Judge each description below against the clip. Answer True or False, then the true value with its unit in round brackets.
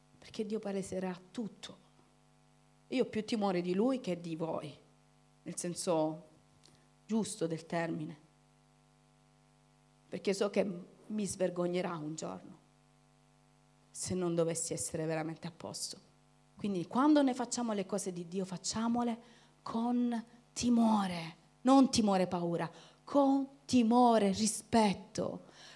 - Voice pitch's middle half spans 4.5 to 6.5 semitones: True (5.2 semitones)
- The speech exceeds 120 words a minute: False (115 wpm)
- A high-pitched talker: True (195 Hz)